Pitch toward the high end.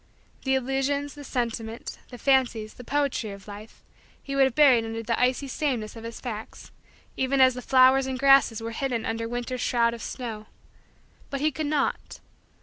Yes: very high, 250 Hz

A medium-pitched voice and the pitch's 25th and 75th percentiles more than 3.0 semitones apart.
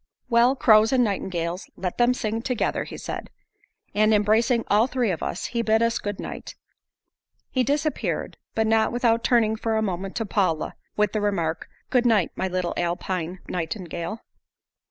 No: high, 215 Hz; average, 3.9 semitones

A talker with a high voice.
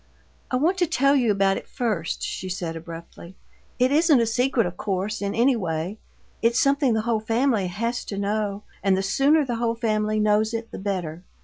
Yes: high, 215 Hz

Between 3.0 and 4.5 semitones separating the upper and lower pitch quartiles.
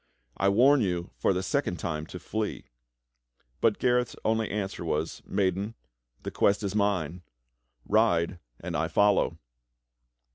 Yes: average, 3.6 semitones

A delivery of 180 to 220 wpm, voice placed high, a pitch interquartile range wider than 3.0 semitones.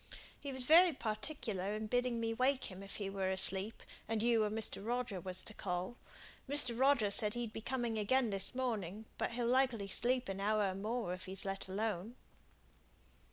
Yes: average, 190 wpm; high, 220 Hz; average, 4.0 semitones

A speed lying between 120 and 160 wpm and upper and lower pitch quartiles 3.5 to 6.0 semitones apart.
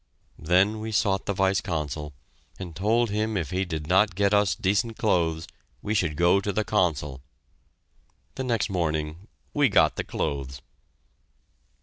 Yes: average, 150 wpm; average, 4.7 semitones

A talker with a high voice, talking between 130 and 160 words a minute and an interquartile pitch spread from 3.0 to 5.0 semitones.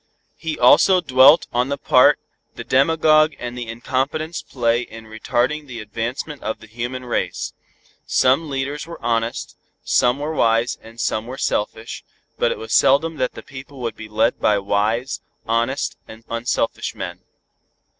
No: low, 125 Hz; average, 155 wpm; average, 3.6 semitones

